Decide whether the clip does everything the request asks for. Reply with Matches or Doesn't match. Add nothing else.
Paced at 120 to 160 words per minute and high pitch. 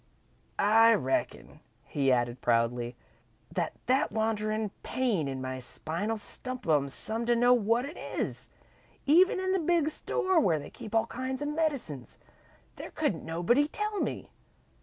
Matches